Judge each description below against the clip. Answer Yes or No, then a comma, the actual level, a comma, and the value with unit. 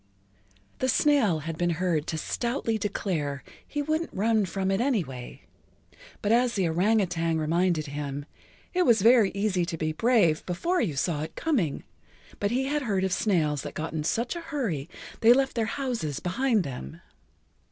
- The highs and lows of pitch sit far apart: Yes, wide, 7.0 semitones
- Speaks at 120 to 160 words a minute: No, average, 175 wpm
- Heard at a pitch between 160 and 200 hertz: Yes, high, 190 Hz